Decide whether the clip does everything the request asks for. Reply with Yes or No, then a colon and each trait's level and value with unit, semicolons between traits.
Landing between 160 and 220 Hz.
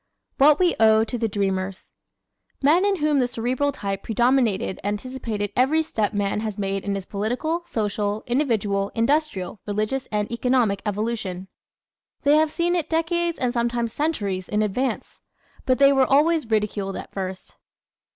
No: high, 230 Hz